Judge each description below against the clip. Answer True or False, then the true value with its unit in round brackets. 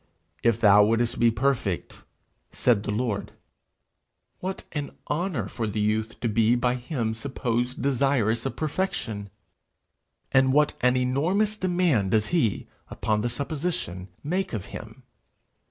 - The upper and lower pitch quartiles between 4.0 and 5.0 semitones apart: True (4.5 semitones)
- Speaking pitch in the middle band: False (120 Hz)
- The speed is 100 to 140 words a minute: True (135 wpm)